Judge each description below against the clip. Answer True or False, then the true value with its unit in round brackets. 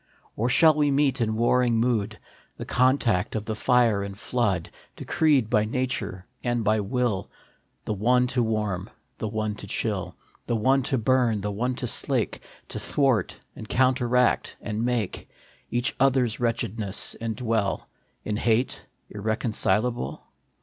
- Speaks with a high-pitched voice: False (115 Hz)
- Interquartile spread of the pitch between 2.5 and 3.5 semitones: True (2.8 semitones)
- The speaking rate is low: False (150 wpm)